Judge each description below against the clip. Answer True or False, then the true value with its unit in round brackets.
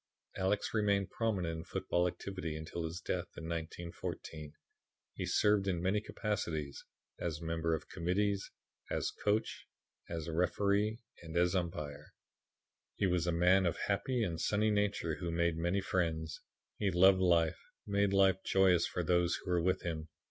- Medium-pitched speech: False (90 Hz)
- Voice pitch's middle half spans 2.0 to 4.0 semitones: True (3.0 semitones)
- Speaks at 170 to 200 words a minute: False (155 wpm)